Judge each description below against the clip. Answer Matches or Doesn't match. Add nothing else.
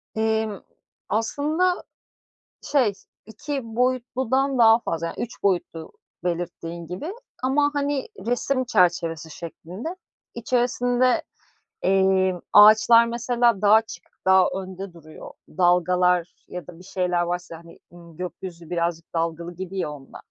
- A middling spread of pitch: Doesn't match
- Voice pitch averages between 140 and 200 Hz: Matches